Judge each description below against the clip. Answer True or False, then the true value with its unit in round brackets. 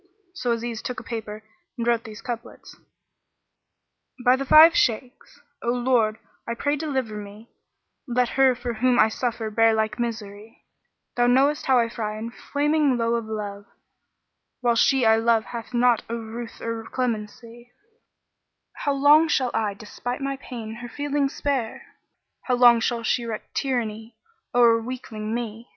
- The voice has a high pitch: True (235 Hz)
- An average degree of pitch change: False (2.3 semitones)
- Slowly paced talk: False (165 wpm)